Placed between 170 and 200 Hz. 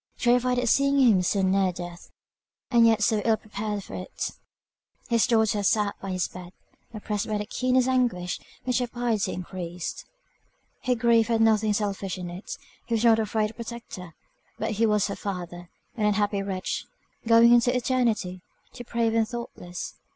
No: high, 215 Hz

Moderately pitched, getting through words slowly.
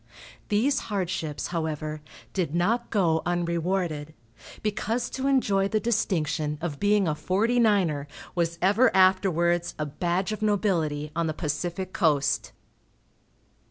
Yes: medium, 175 Hz; slow, 125 wpm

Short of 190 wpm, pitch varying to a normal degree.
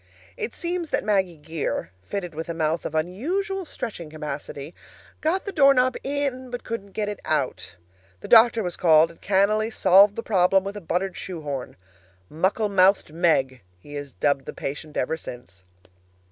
No: average, 170 wpm; wide, 6.5 semitones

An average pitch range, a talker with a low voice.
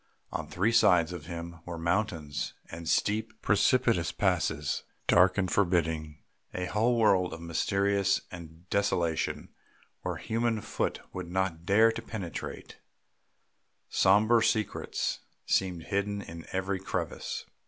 Yes: average, 3.6 semitones; very low, 95 Hz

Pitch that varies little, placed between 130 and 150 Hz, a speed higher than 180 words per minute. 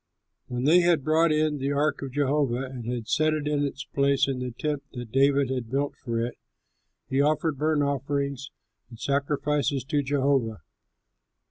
No: narrow, 2.2 semitones; medium, 140 Hz; average, 170 wpm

